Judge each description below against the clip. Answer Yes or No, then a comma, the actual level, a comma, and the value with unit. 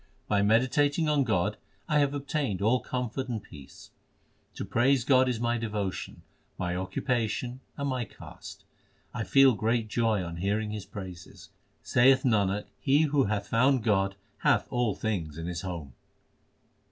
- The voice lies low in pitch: Yes, low, 115 Hz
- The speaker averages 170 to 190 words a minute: No, average, 155 wpm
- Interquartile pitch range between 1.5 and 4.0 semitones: No, average, 4.8 semitones